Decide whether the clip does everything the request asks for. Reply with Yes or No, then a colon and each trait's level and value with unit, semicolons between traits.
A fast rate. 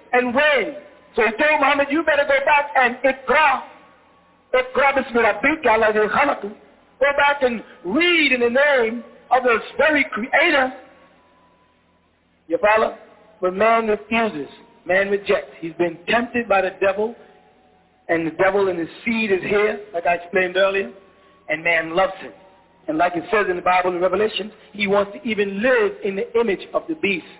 No: average, 160 wpm